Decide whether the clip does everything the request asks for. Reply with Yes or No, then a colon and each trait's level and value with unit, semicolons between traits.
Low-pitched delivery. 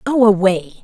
No: high, 215 Hz